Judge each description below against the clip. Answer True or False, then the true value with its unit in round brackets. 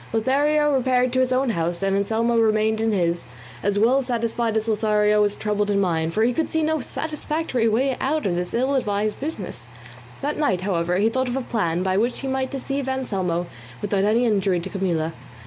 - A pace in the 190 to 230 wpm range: True (200 wpm)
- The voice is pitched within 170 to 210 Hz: False (220 Hz)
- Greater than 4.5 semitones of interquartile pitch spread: True (4.9 semitones)